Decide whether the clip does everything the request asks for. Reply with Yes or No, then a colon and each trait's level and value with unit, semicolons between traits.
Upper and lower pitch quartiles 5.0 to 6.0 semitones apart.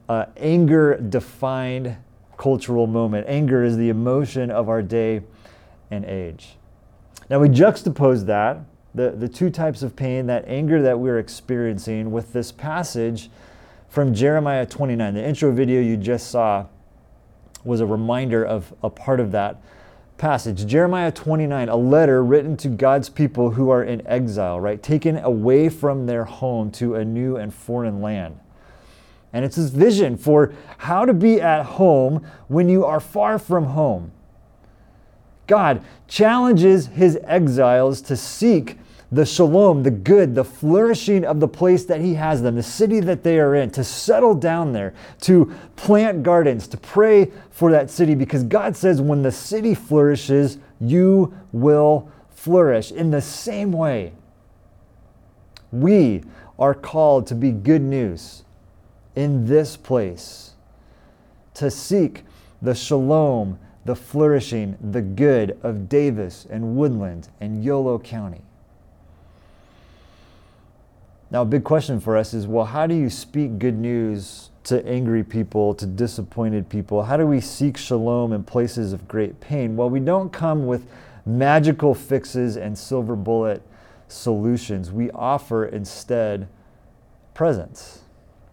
Yes: wide, 5.4 semitones